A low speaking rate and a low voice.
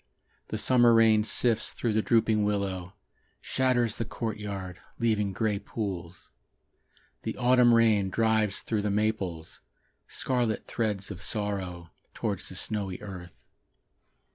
Yes: slow, 120 wpm; low, 105 Hz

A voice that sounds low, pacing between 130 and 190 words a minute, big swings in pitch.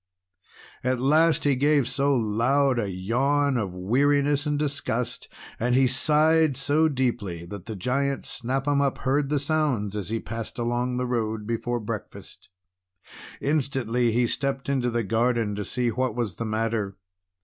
No: low, 125 Hz; average, 160 wpm; average, 3.7 semitones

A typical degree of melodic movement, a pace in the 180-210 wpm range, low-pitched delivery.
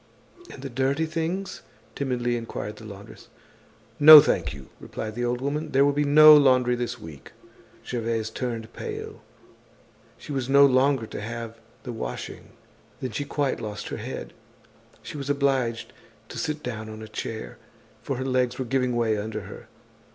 No: average, 3.8 semitones; average, 165 wpm; low, 125 Hz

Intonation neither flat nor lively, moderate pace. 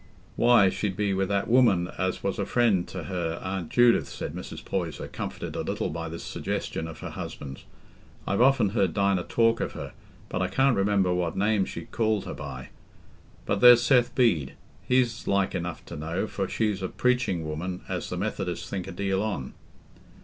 Yes: average, 4.4 semitones; average, 190 wpm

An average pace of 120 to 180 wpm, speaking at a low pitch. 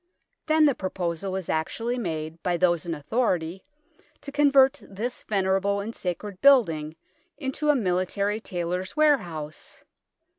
No: slow, 135 wpm; high, 190 Hz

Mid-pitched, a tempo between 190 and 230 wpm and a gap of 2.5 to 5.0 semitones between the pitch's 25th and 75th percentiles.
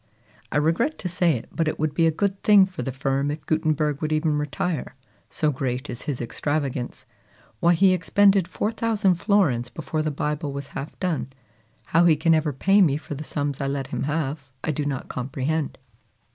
Yes: medium, 155 Hz; average, 195 wpm; average, 3.7 semitones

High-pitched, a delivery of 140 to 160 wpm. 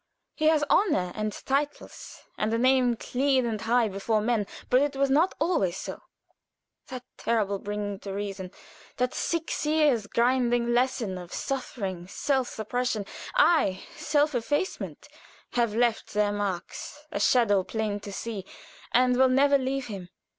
Yes: high, 240 Hz; average, 145 wpm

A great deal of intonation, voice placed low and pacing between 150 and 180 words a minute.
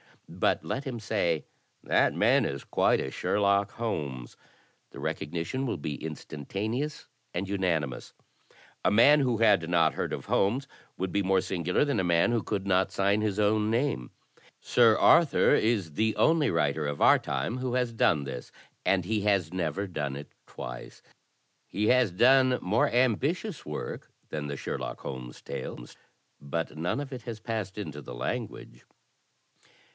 Yes: wide, 6.6 semitones; low, 100 Hz; average, 160 wpm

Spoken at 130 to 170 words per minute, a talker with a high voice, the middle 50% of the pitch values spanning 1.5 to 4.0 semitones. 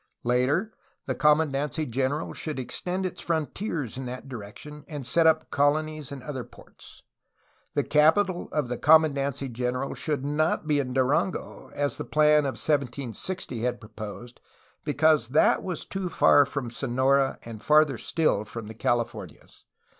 No: average, 150 wpm; medium, 140 Hz; average, 3.7 semitones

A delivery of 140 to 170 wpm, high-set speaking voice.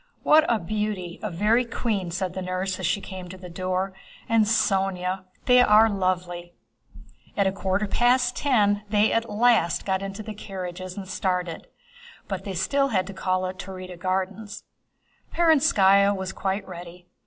Yes: average, 165 wpm; high, 195 Hz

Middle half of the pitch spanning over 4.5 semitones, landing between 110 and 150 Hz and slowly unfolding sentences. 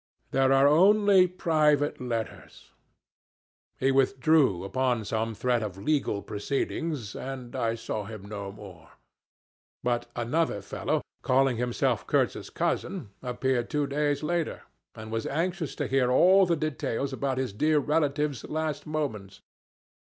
Yes: average, 5.1 semitones; low, 135 Hz; slow, 130 wpm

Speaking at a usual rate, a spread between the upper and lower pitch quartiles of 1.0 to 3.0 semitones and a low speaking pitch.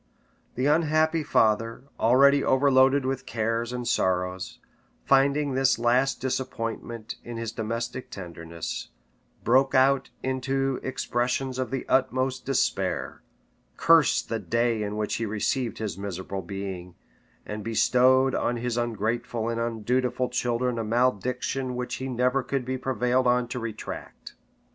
No: slow, 130 wpm; narrow, 2.6 semitones; low, 125 Hz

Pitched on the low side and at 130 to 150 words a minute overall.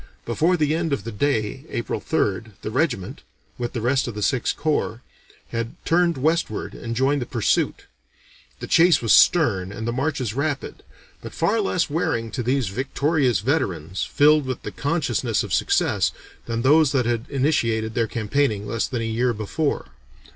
No: low, 125 Hz; average, 170 wpm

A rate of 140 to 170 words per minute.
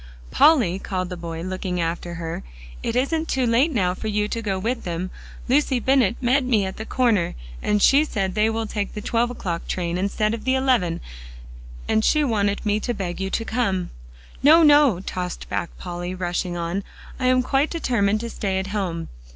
No: average, 195 wpm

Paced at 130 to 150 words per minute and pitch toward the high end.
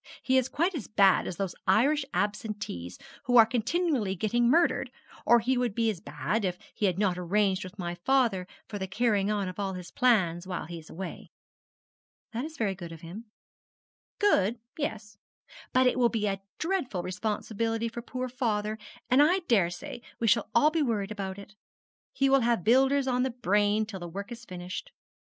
No: average, 190 wpm; high, 215 Hz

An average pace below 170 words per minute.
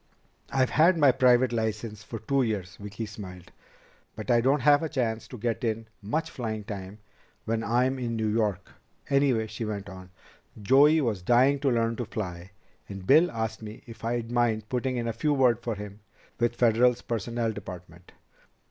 No: average, 180 wpm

